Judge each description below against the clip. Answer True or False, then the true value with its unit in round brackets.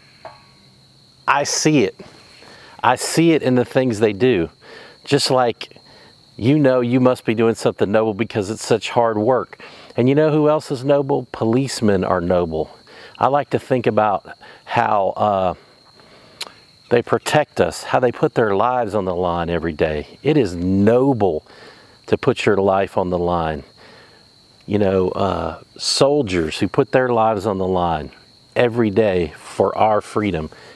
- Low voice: True (110 Hz)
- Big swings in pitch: True (5.7 semitones)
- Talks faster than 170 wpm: False (160 wpm)